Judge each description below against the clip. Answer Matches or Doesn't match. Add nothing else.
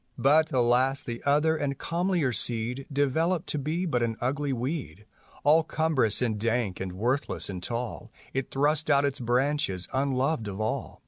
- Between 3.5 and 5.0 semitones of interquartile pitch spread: Matches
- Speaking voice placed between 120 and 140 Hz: Matches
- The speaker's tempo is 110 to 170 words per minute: Matches